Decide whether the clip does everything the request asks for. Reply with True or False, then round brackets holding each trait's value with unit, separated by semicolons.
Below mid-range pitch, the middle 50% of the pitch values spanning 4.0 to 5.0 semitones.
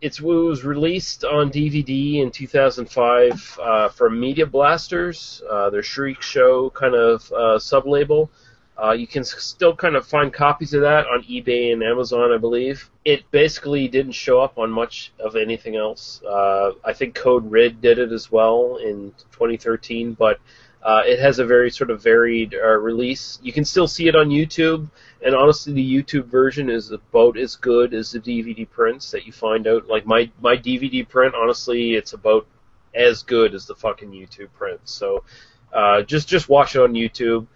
True (125 Hz; 4.5 semitones)